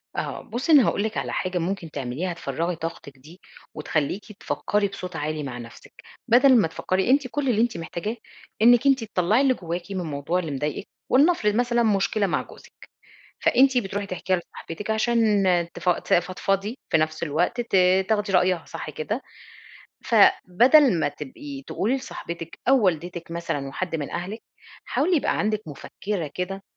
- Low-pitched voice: No, medium, 185 Hz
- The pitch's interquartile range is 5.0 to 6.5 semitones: Yes, wide, 5.4 semitones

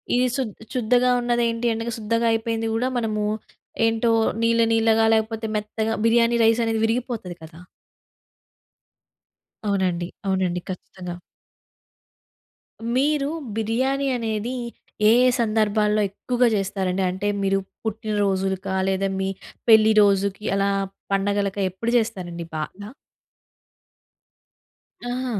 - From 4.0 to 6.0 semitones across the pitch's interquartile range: No, average, 2.8 semitones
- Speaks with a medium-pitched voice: No, high, 220 Hz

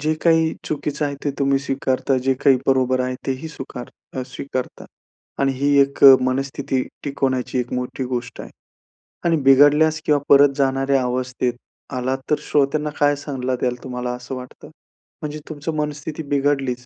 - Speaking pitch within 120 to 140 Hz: Yes, low, 135 Hz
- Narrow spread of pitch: Yes, narrow, 2.2 semitones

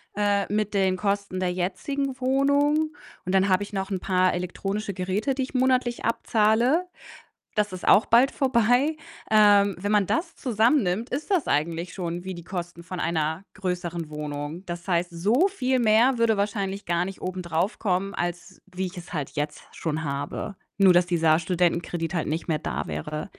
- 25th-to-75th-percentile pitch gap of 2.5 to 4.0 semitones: No, average, 4.4 semitones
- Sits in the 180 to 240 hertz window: Yes, high, 190 Hz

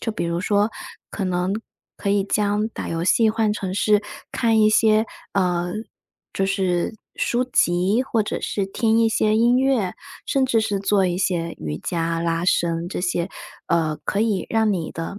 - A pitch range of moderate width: Yes, average, 3.9 semitones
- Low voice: No, high, 200 Hz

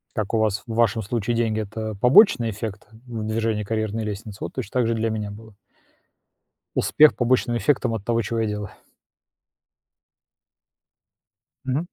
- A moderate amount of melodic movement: No, narrow, 1.7 semitones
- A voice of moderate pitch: No, low, 110 Hz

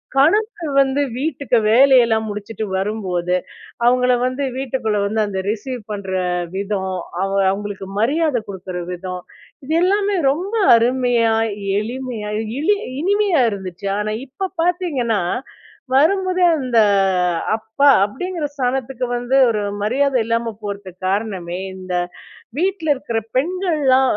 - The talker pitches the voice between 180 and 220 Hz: No, high, 245 Hz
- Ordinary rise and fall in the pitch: No, wide, 5.7 semitones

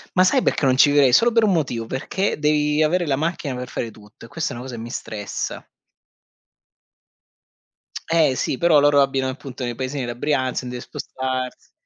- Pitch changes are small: No, average, 3.4 semitones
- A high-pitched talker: No, low, 135 Hz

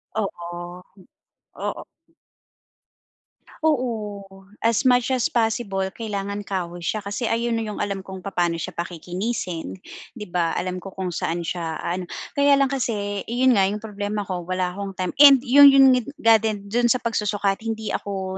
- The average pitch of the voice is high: Yes, high, 205 Hz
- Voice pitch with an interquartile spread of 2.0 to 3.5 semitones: No, average, 3.9 semitones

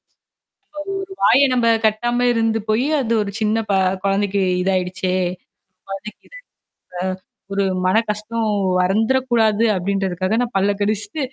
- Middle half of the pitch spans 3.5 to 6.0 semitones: No, average, 2.9 semitones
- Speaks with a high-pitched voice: Yes, high, 215 Hz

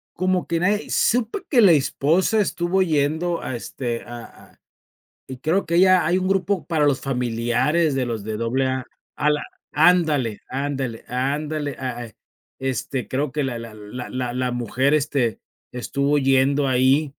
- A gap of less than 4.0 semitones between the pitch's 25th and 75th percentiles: No, average, 4.8 semitones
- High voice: No, medium, 140 Hz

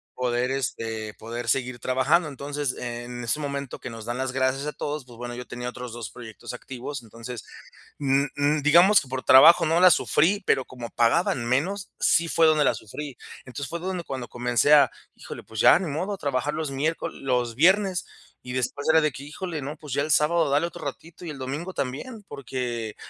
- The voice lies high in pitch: No, low, 135 Hz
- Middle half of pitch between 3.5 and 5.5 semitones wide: Yes, average, 4.0 semitones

